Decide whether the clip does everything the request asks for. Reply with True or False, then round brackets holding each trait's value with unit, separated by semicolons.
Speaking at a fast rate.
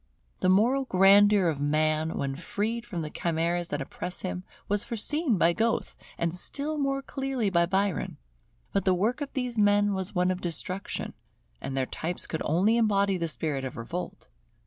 False (175 wpm)